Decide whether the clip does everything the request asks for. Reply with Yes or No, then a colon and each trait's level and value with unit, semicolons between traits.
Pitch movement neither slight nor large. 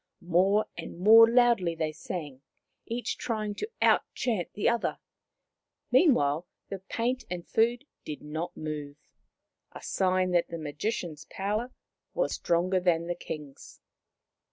No: wide, 5.8 semitones